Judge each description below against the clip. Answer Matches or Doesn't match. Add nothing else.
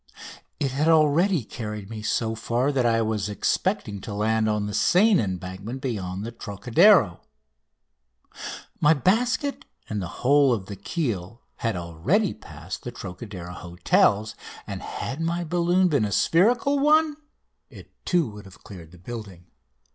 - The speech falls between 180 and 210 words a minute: Doesn't match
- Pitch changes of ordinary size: Doesn't match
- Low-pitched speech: Matches